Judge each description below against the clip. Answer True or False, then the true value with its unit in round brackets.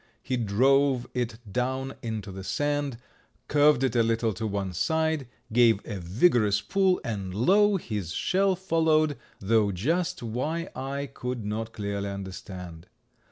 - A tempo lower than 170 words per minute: True (140 wpm)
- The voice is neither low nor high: False (120 Hz)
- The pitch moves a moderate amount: False (6.2 semitones)